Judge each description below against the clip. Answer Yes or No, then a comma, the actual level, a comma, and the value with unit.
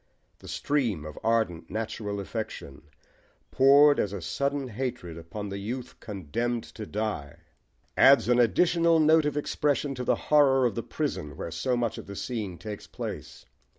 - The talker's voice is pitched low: Yes, low, 115 Hz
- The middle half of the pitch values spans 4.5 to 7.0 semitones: Yes, wide, 5.4 semitones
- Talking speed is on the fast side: No, average, 155 wpm